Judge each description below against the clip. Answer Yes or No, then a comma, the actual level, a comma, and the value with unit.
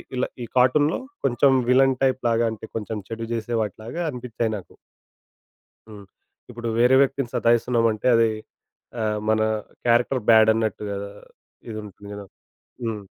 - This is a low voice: Yes, low, 115 Hz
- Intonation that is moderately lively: No, narrow, 2.3 semitones